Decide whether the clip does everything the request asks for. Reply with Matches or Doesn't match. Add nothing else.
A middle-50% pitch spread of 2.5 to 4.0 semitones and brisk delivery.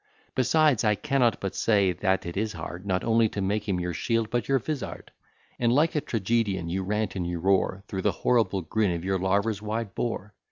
Matches